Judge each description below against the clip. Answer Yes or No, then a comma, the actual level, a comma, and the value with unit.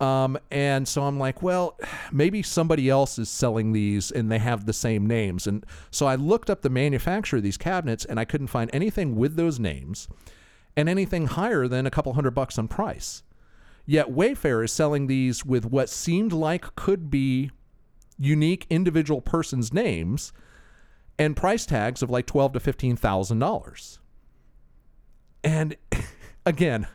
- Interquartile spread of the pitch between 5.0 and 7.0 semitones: Yes, average, 5.3 semitones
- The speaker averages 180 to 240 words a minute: No, average, 160 wpm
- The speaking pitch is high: No, low, 135 Hz